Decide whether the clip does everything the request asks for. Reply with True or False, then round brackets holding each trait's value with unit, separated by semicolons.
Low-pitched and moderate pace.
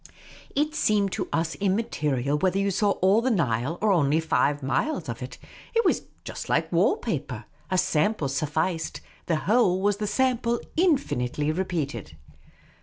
False (185 Hz; 160 wpm)